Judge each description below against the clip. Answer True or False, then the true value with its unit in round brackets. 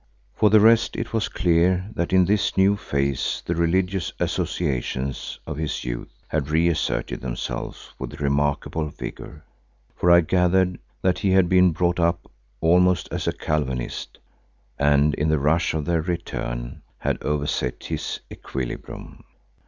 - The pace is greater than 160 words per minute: False (145 wpm)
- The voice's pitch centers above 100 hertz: False (85 Hz)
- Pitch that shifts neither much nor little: True (4.0 semitones)